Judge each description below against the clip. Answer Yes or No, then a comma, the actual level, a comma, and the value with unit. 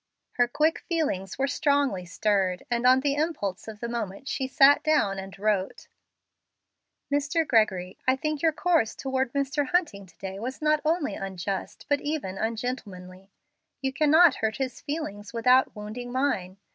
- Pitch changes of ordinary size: No, wide, 6.6 semitones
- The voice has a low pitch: No, very high, 250 Hz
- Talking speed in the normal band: Yes, average, 160 wpm